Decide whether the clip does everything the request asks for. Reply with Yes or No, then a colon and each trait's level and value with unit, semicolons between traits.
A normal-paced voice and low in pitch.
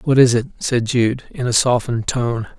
No: fast, 210 wpm; low, 120 Hz